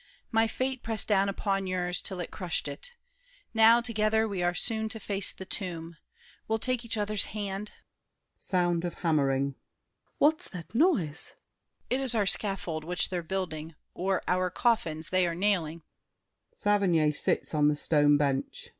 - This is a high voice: Yes, high, 195 Hz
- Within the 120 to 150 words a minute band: Yes, average, 145 wpm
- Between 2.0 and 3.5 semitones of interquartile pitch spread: No, average, 4.1 semitones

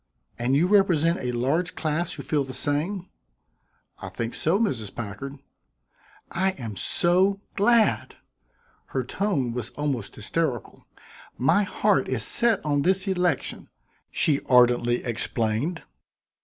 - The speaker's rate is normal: No, slow, 125 wpm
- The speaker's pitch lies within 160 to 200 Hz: No, medium, 150 Hz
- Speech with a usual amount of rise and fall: No, wide, 7.0 semitones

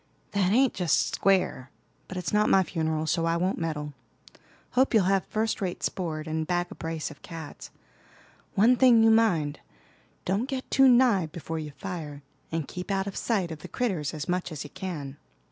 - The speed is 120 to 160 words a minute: No, average, 190 wpm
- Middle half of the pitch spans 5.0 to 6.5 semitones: No, average, 4.4 semitones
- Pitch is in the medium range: Yes, medium, 180 Hz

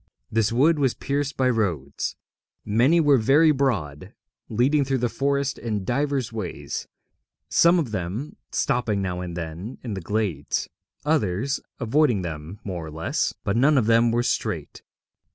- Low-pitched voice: Yes, low, 115 Hz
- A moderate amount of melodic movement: No, wide, 6.7 semitones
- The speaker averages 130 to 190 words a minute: Yes, average, 150 wpm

